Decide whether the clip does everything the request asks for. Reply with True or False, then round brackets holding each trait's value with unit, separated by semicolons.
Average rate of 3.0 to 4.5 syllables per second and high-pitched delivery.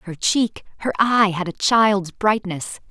True (3.7 syllables/s; 200 Hz)